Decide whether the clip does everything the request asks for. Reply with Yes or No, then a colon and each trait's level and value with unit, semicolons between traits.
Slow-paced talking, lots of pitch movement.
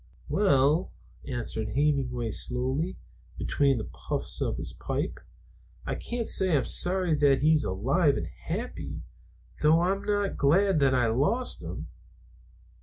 Yes: slow, 130 wpm; wide, 6.1 semitones